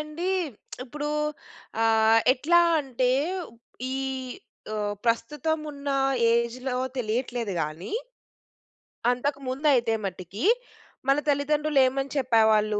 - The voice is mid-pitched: No, very high, 250 Hz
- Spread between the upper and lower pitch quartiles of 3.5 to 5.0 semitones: Yes, average, 4.2 semitones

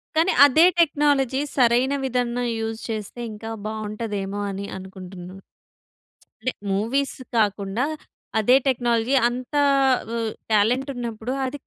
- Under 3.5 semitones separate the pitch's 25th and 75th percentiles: No, average, 3.8 semitones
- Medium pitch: No, high, 235 Hz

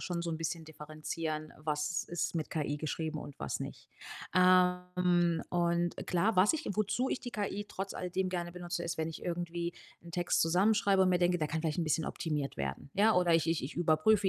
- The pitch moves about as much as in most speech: No, narrow, 2.3 semitones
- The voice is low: No, medium, 175 Hz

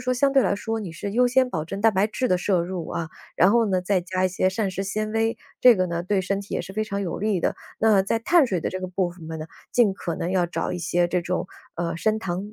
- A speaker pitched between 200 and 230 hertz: No, high, 190 Hz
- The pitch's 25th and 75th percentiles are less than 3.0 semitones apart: No, average, 3.5 semitones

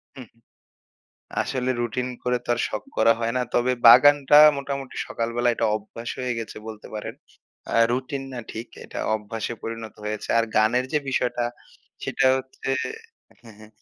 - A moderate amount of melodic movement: No, narrow, 2.3 semitones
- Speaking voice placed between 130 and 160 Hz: No, low, 120 Hz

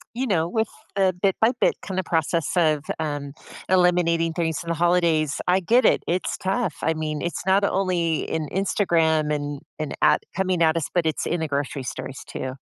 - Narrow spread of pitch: No, average, 3.2 semitones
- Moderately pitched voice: Yes, medium, 170 Hz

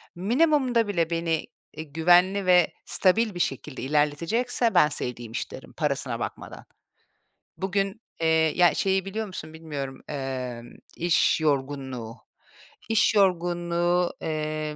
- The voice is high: No, medium, 170 Hz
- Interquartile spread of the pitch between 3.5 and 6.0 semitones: Yes, average, 4.6 semitones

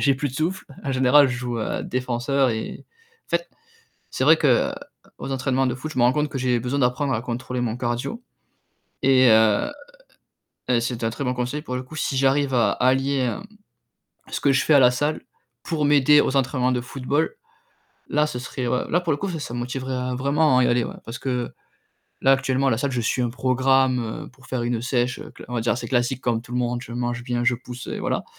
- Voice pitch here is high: No, low, 130 Hz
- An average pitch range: No, narrow, 2.0 semitones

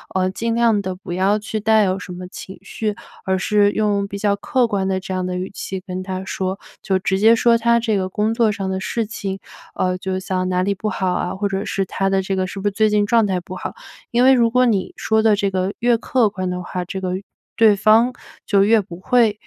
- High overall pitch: Yes, high, 200 Hz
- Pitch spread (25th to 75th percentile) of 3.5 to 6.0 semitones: No, average, 2.7 semitones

